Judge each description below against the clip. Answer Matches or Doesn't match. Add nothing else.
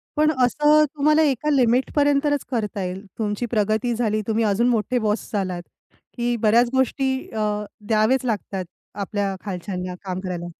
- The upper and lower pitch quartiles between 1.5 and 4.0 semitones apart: Doesn't match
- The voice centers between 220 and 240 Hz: Matches